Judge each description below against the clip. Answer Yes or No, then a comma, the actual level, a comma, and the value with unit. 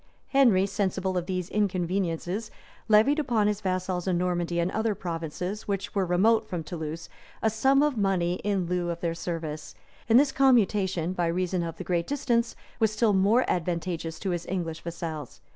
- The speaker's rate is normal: Yes, average, 175 wpm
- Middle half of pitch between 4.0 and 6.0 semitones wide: No, average, 3.6 semitones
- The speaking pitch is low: No, medium, 185 Hz